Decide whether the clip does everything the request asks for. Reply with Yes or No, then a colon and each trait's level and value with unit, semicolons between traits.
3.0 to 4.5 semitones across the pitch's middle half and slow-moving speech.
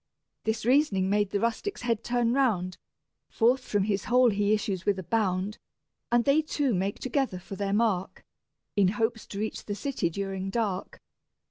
No: average, 3.7 semitones; average, 170 wpm